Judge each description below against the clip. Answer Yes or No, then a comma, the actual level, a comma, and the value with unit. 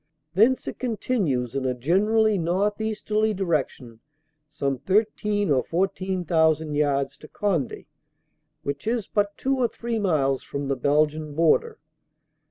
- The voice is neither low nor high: Yes, medium, 175 Hz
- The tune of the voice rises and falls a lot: Yes, wide, 6.8 semitones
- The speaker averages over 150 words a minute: No, slow, 135 wpm